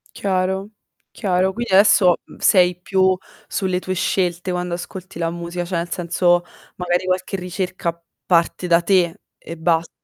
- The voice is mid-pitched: Yes, medium, 180 Hz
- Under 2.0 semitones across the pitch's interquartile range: Yes, narrow, 1.5 semitones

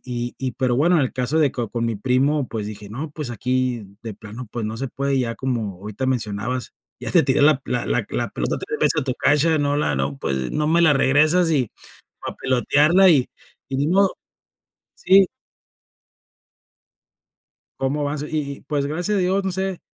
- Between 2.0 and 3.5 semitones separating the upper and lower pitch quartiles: No, average, 4.3 semitones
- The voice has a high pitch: No, low, 135 Hz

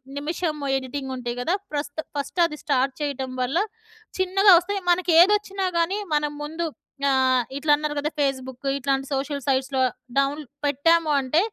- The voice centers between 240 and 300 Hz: Yes, very high, 290 Hz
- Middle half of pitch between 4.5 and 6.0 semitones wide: No, average, 3.8 semitones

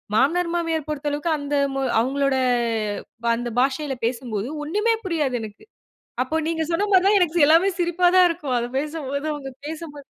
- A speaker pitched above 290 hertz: Yes, very high, 300 Hz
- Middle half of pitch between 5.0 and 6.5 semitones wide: No, average, 4.0 semitones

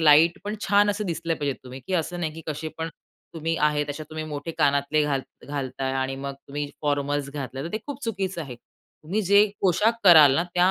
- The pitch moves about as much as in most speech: Yes, average, 3.7 semitones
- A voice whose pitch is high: No, medium, 155 Hz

